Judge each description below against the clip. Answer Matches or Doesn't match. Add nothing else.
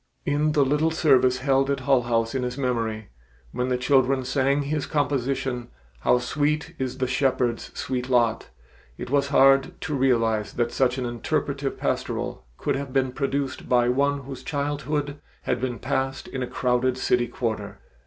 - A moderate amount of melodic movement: Doesn't match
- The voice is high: Doesn't match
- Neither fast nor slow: Matches